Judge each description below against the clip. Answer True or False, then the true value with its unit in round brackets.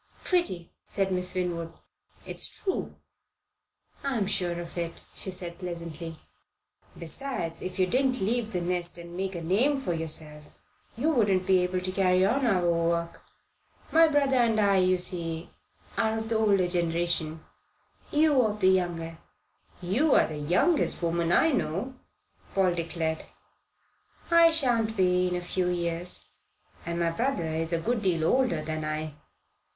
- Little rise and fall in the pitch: False (4.7 semitones)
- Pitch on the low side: False (180 Hz)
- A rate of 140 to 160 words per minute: True (150 wpm)